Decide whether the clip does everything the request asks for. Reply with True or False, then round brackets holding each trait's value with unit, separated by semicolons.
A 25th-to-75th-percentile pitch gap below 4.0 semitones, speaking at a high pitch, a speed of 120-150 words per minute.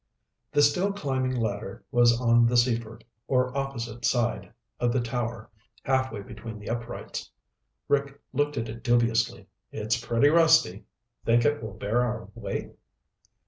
False (2.5 semitones; 120 Hz; 140 wpm)